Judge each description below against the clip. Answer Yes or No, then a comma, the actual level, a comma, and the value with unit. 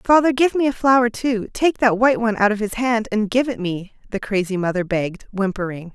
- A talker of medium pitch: No, high, 220 Hz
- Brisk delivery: Yes, fast, 230 wpm